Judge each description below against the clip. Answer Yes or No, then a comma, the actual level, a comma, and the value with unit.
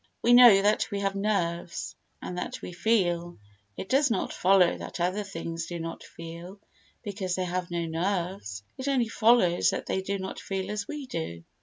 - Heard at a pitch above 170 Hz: Yes, high, 190 Hz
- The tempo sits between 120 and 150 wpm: No, average, 180 wpm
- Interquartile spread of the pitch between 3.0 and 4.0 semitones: Yes, average, 3.5 semitones